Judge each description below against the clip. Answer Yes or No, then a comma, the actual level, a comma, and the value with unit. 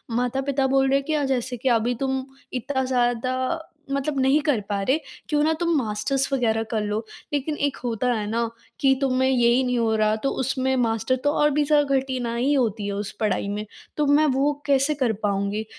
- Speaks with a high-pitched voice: Yes, very high, 260 Hz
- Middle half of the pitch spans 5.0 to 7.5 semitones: No, average, 3.4 semitones